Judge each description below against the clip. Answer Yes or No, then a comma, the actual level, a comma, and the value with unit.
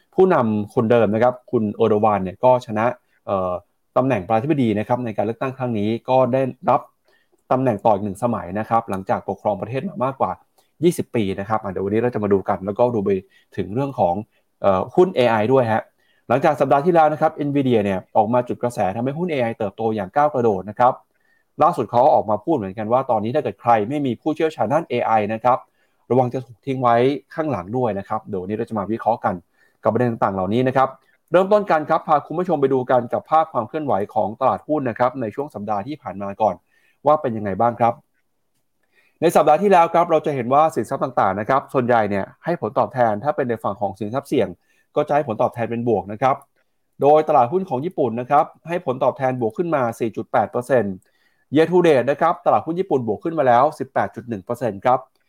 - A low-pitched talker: Yes, low, 125 Hz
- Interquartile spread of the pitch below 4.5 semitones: No, average, 4.9 semitones